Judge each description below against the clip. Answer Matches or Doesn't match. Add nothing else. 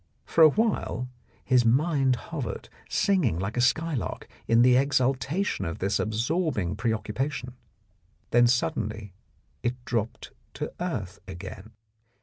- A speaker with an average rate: Doesn't match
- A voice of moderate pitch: Doesn't match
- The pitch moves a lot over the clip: Doesn't match